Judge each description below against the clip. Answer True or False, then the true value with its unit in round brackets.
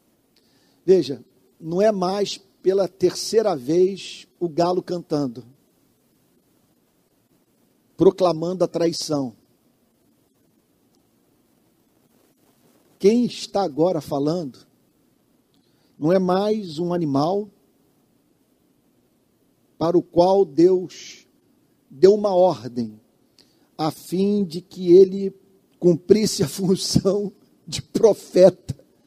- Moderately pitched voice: True (180 Hz)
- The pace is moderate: False (80 wpm)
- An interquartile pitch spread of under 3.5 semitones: True (2.7 semitones)